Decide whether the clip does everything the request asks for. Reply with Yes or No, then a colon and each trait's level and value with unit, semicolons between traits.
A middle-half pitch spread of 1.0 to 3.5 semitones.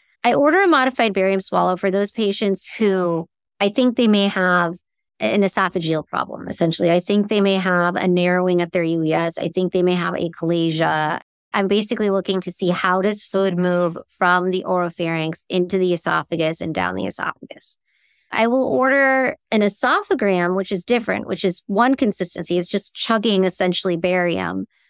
Yes: average, 2.7 semitones